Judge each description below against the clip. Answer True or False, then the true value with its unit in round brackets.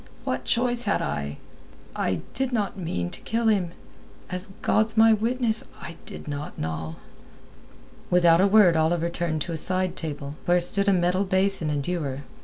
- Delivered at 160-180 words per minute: True (165 wpm)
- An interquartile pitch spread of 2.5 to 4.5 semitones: False (5.1 semitones)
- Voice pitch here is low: False (180 Hz)